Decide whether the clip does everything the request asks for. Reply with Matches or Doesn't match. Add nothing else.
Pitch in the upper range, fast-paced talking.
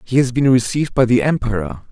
Doesn't match